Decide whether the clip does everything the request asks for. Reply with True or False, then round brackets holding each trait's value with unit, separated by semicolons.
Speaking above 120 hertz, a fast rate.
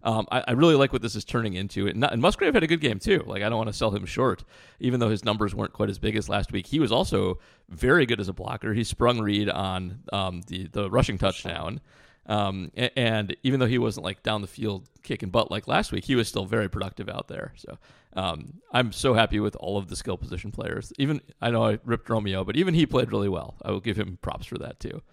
False (110 Hz; 260 wpm)